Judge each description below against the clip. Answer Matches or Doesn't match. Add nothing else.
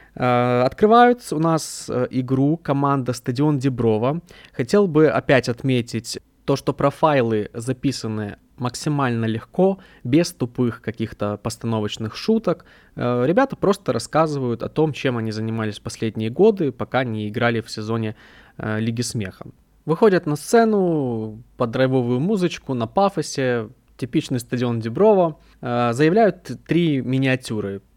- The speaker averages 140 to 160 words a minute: Doesn't match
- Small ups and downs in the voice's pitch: Doesn't match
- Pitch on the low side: Matches